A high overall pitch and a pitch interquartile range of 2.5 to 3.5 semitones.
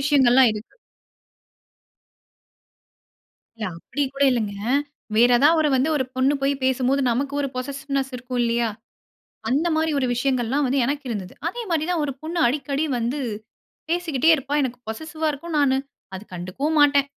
Yes: very high, 275 Hz; average, 2.9 semitones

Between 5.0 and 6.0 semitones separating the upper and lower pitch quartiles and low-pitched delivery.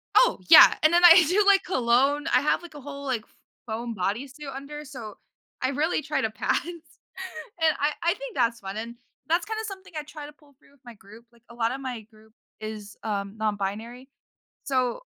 No: wide, 5.6 semitones; very high, 270 Hz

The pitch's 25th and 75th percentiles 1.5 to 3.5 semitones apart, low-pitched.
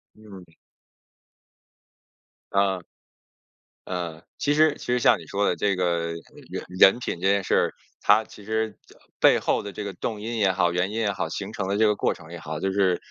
Yes: average, 3.0 semitones; low, 100 Hz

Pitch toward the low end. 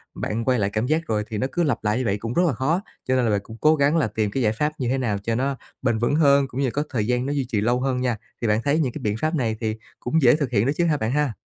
Yes: low, 125 Hz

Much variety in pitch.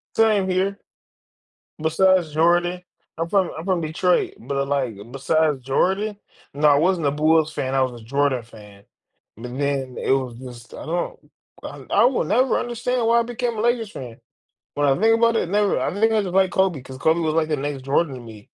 Yes: wide, 6.1 semitones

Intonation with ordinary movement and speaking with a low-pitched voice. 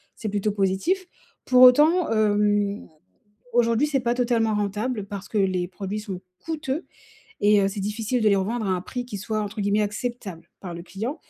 No: average, 3.4 semitones; high, 210 Hz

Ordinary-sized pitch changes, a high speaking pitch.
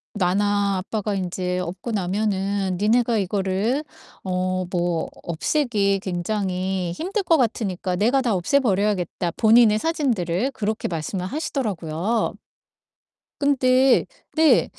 Yes: average, 4.4 semitones; high, 200 Hz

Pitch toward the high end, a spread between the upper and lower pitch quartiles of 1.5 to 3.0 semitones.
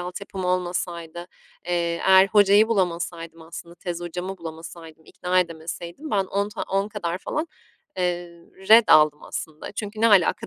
No: medium, 180 Hz; average, 2.7 semitones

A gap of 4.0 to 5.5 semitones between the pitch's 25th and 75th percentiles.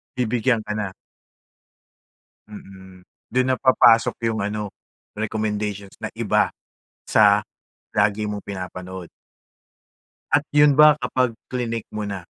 No: average, 3.6 semitones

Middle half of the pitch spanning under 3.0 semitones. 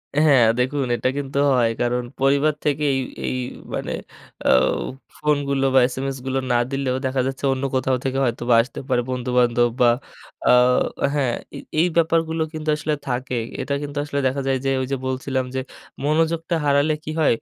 Yes: narrow, 2.5 semitones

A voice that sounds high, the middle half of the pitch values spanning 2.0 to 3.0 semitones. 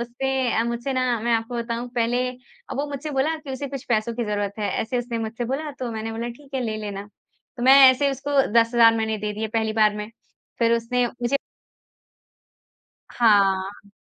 Yes: high, 235 Hz; narrow, 2.5 semitones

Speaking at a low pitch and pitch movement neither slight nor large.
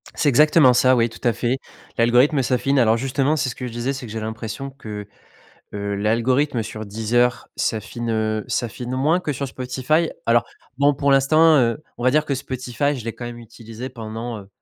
Yes: low, 125 Hz; average, 3.2 semitones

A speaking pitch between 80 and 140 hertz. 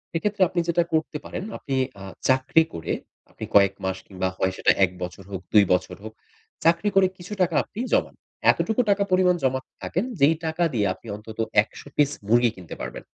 Yes: low, 135 Hz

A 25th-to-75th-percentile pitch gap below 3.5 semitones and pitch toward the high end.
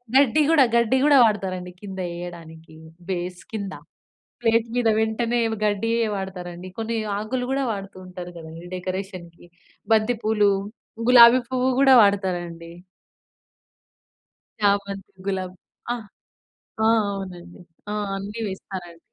No: average, 4.0 semitones; high, 195 Hz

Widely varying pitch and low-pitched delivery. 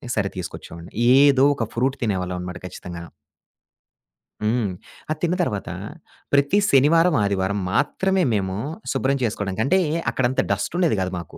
Yes: wide, 6.9 semitones; low, 110 Hz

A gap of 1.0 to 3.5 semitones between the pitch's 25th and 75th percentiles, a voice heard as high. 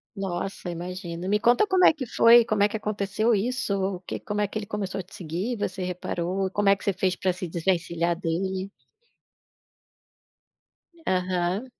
Yes: narrow, 2.6 semitones; high, 195 Hz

